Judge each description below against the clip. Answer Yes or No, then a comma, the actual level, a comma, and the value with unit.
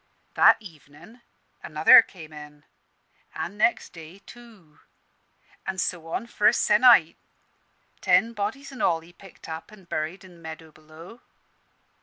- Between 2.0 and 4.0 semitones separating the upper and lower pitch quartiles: No, average, 4.9 semitones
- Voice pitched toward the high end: No, medium, 175 Hz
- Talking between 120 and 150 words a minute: Yes, average, 140 wpm